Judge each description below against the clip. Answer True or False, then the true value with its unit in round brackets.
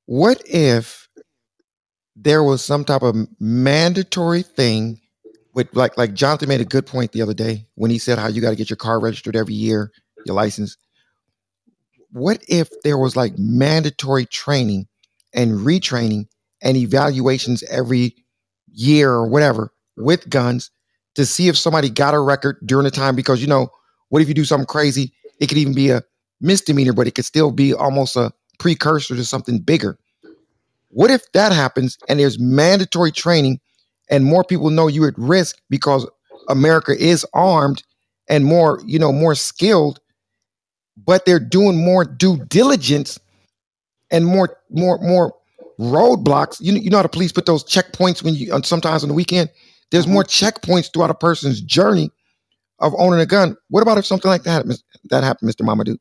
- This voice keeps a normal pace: True (175 wpm)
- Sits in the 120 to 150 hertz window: True (140 Hz)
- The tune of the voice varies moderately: False (5.8 semitones)